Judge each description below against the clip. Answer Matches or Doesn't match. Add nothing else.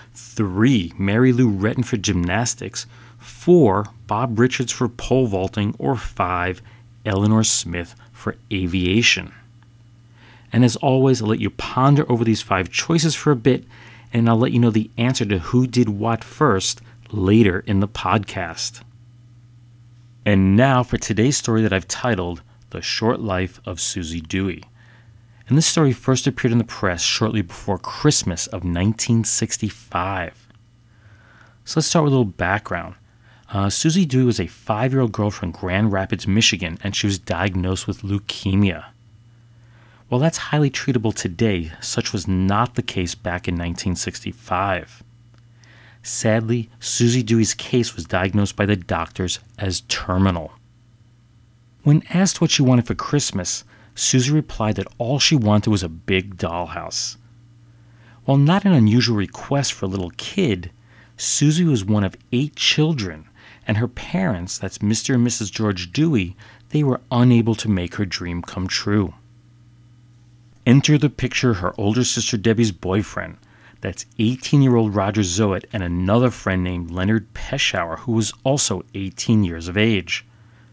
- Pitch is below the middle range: Matches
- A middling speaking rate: Matches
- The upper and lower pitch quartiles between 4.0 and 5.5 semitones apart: Doesn't match